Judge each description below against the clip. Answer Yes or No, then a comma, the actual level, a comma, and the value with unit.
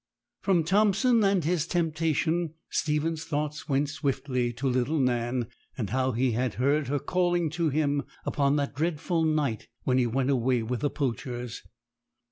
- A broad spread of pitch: No, average, 4.2 semitones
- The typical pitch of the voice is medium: Yes, medium, 145 Hz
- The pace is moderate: Yes, average, 155 wpm